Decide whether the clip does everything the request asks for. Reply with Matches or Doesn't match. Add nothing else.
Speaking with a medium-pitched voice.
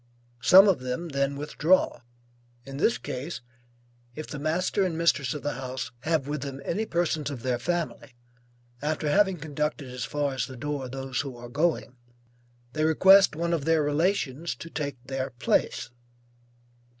Matches